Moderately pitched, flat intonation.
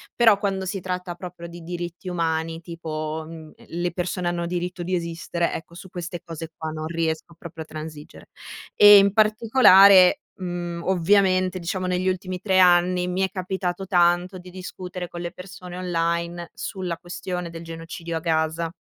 Yes: medium, 175 Hz; narrow, 1.7 semitones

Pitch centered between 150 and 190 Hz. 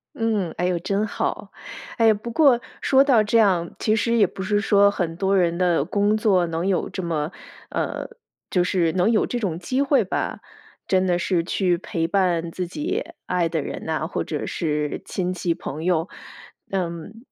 Yes: medium, 185 Hz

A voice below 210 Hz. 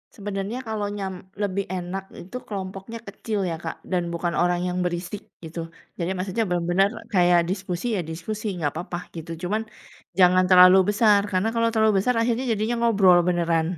Yes: high, 190 Hz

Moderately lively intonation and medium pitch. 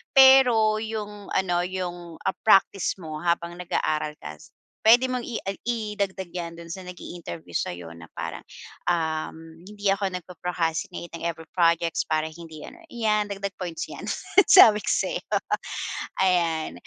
Yes: average, 4.2 semitones; medium, 180 Hz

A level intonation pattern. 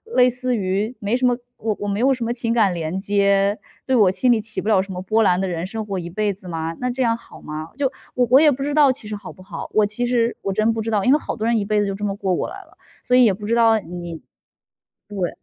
No: average, 3.8 semitones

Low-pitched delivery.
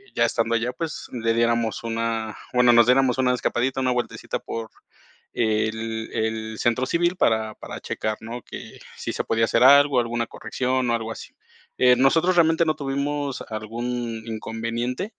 Yes: low, 120 Hz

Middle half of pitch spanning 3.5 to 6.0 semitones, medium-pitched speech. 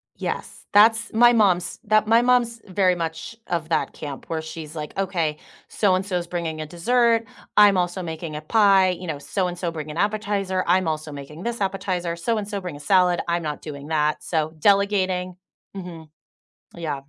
Yes: average, 4.1 semitones; medium, 180 Hz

